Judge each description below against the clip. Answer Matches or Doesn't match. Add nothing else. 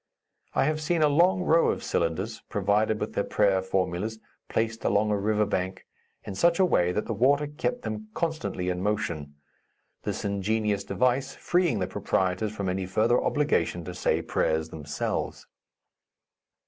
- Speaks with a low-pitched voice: Matches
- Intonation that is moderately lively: Doesn't match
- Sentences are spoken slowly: Doesn't match